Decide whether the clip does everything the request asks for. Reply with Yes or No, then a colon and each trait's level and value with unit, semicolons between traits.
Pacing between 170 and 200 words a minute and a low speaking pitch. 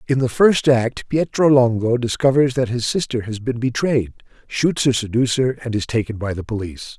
Yes: average, 190 wpm; low, 125 Hz